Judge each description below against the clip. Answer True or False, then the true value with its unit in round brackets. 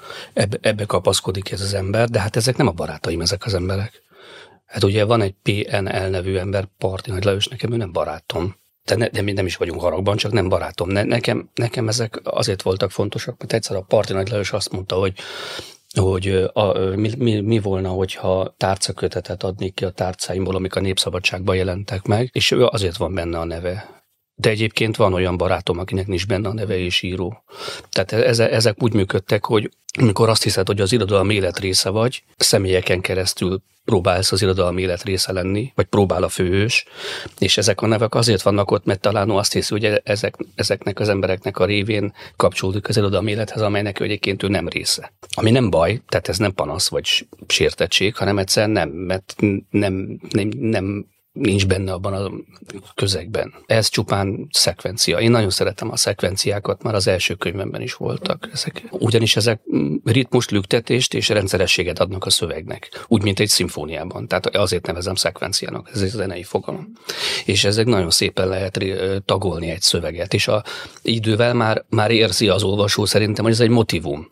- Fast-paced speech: True (180 wpm)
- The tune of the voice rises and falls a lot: False (2.8 semitones)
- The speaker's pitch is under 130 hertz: True (100 Hz)